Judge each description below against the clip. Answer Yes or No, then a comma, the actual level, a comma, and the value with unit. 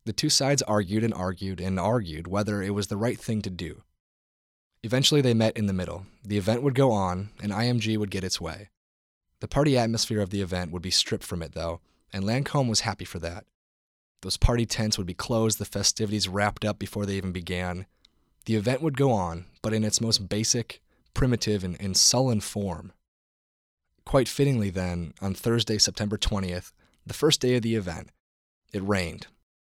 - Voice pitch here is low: Yes, low, 105 Hz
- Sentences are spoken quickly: No, average, 190 wpm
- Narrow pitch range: No, average, 3.8 semitones